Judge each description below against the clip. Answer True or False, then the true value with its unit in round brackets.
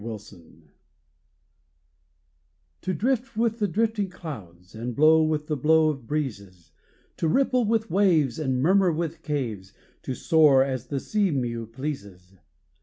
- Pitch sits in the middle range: True (150 Hz)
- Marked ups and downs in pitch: True (8.0 semitones)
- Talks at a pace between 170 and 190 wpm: False (135 wpm)